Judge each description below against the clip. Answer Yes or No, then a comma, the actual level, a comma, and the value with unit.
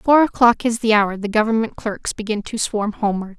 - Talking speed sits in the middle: No, fast, 215 wpm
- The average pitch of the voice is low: No, high, 220 Hz